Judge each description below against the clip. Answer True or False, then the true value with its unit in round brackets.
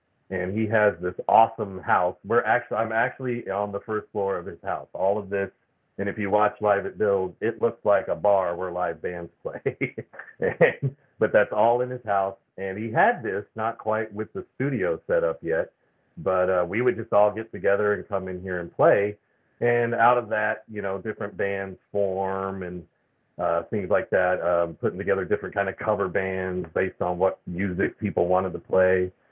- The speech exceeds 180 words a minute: True (205 wpm)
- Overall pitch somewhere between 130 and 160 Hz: False (100 Hz)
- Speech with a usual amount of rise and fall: True (3.1 semitones)